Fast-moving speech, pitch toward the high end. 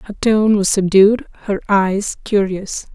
No: average, 145 wpm; high, 200 Hz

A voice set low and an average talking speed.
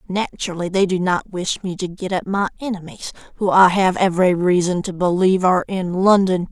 No: medium, 185 Hz; average, 195 wpm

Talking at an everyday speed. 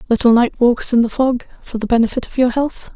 No: fast, 245 wpm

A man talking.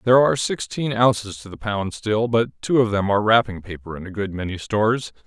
Yes: male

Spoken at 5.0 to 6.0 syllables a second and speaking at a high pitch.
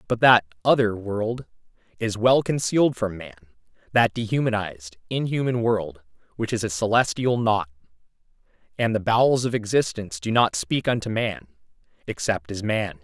No: 5.1 syllables/s; low, 110 Hz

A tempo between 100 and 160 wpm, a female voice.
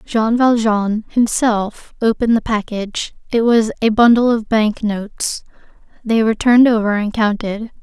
Yes: average, 145 wpm; female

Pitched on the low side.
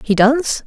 No: very high, 250 Hz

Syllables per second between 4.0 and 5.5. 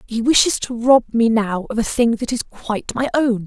Yes: 5.0 syllables/s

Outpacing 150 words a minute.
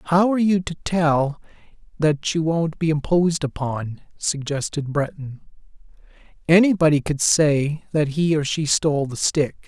No: average, 145 wpm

